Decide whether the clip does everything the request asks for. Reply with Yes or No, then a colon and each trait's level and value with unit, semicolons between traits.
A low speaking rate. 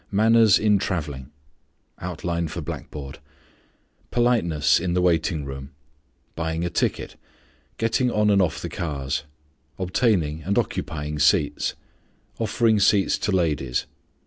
Yes: slow, 105 wpm